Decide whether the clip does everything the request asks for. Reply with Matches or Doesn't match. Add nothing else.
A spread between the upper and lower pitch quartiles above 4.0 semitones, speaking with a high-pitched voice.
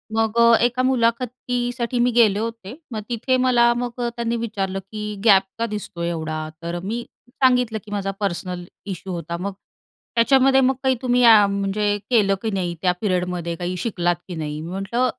Matches